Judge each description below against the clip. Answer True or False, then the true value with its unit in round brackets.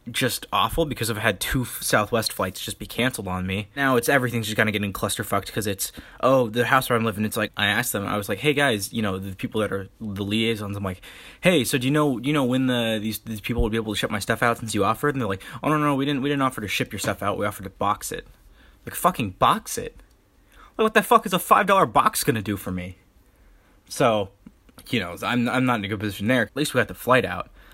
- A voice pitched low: True (115 Hz)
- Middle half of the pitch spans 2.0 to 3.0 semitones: False (4.0 semitones)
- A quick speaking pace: True (280 wpm)